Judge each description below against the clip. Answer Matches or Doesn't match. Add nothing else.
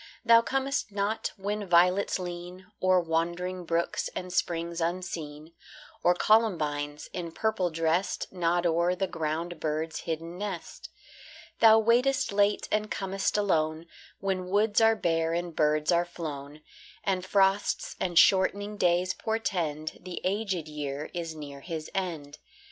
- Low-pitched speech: Doesn't match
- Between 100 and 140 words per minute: Matches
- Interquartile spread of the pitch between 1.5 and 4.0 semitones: Matches